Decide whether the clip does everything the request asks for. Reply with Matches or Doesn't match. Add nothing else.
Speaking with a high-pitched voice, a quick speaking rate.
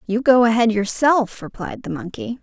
Doesn't match